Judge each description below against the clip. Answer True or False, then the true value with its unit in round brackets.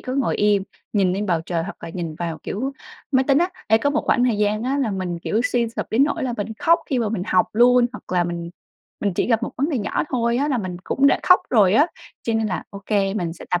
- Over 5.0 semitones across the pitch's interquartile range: True (5.4 semitones)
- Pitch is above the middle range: True (225 Hz)